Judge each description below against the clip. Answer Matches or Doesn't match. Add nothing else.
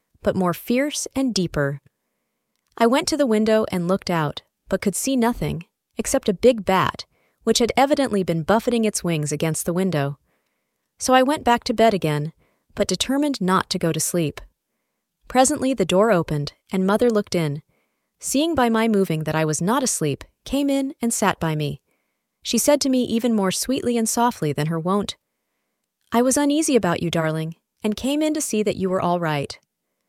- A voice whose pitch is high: Matches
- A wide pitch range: Matches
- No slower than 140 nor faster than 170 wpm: Doesn't match